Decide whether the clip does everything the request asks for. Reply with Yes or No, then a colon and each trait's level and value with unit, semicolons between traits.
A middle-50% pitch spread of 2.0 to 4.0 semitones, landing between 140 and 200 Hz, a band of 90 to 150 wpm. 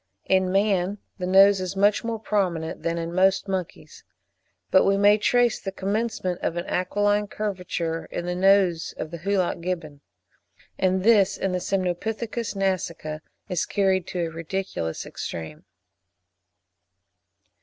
Yes: narrow, 2.6 semitones; high, 190 Hz; average, 140 wpm